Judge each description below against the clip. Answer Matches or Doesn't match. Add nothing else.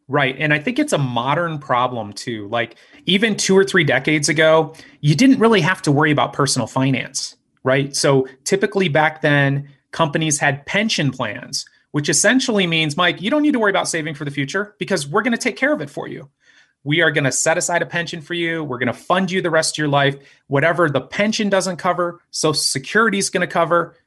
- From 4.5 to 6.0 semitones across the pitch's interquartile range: Matches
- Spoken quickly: Matches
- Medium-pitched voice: Matches